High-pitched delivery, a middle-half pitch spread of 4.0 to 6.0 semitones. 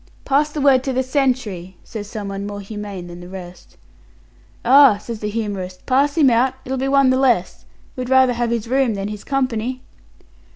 Yes: high, 235 Hz; average, 4.5 semitones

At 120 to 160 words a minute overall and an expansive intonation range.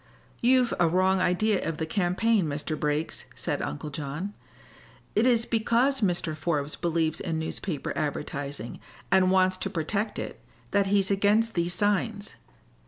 No: average, 145 wpm; average, 4.6 semitones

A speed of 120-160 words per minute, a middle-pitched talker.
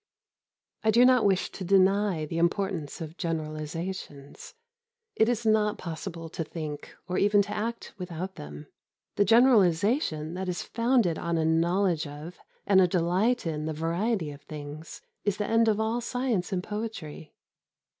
Yes: average, 155 wpm; medium, 180 Hz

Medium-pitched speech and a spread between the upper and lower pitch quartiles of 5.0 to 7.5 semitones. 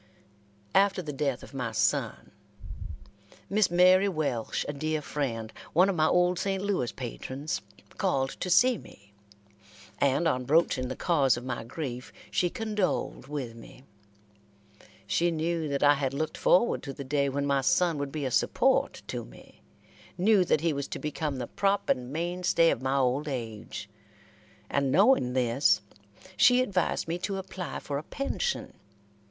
Yes: medium, 150 Hz; wide, 5.4 semitones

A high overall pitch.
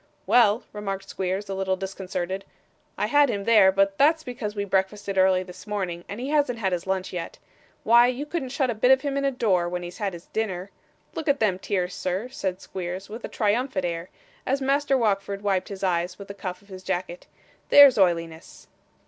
Yes: high, 195 Hz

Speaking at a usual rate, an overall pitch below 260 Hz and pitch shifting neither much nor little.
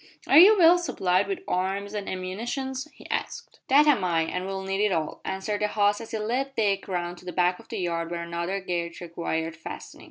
No: fast, 220 wpm; high, 190 Hz; average, 3.6 semitones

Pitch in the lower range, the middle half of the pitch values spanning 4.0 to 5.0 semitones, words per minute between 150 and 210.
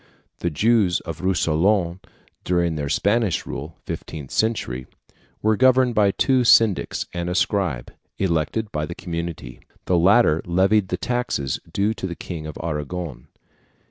No: very low, 90 Hz; average, 4.7 semitones; average, 140 wpm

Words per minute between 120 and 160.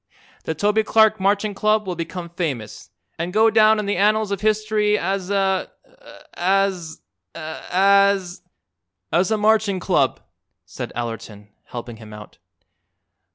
Yes: slow, 135 wpm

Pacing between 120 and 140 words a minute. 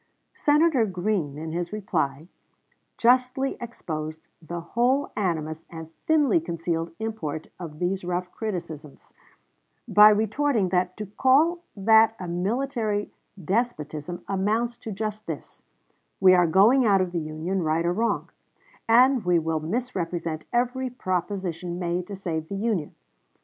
Yes: slow, 135 wpm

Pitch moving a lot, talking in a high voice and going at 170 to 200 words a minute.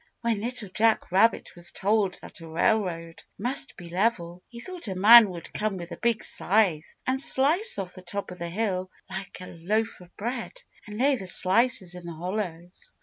No: average, 4.5 semitones; high, 200 Hz; average, 195 wpm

